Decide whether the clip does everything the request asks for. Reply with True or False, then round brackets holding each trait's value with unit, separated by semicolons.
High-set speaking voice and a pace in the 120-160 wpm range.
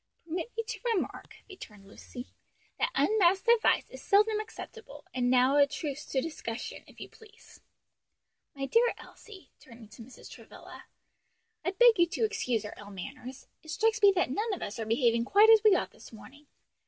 False (315 Hz; 180 wpm)